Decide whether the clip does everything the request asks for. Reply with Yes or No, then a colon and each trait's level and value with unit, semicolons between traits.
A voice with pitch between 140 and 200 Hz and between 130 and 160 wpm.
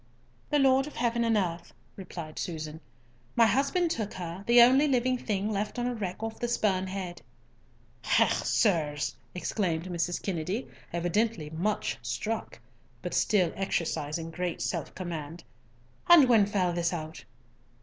Yes: high, 190 Hz; average, 145 wpm